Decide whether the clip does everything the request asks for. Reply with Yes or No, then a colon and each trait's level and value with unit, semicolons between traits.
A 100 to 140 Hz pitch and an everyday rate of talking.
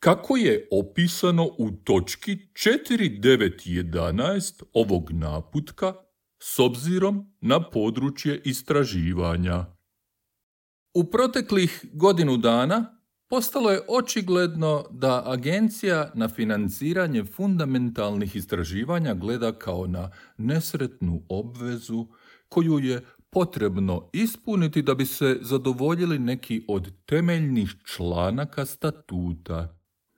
No: low, 135 Hz; slow, 85 wpm